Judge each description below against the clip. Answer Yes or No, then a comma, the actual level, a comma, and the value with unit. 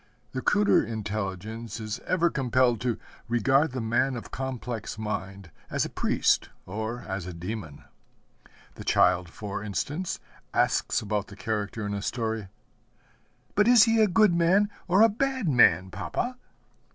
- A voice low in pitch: Yes, low, 115 Hz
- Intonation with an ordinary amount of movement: No, wide, 7.9 semitones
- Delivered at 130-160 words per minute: Yes, average, 150 wpm